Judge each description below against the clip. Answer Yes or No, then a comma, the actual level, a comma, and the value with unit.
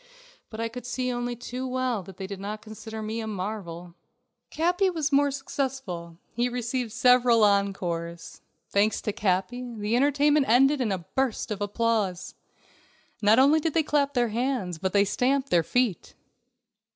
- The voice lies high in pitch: Yes, high, 230 Hz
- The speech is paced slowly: No, average, 165 wpm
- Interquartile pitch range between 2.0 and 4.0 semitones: No, average, 4.5 semitones